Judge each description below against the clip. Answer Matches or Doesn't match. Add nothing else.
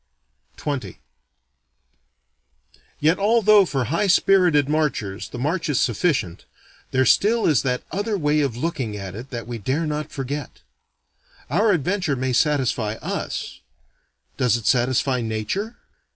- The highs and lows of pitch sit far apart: Matches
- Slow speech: Matches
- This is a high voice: Doesn't match